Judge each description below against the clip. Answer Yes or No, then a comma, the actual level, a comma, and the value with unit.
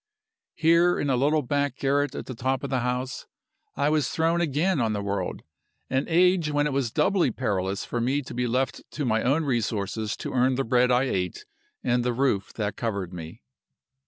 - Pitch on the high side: No, low, 130 Hz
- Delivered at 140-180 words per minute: No, average, 200 wpm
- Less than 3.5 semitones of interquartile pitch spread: No, average, 4.3 semitones